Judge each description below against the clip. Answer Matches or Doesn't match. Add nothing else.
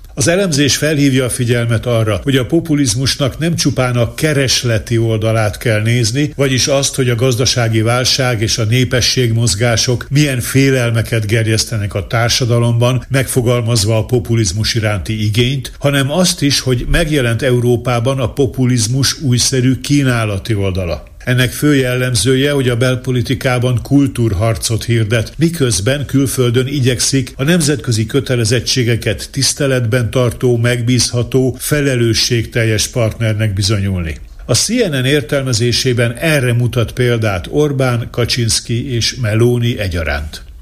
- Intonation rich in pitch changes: Doesn't match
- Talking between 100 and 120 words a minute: Matches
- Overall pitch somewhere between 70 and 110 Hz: Doesn't match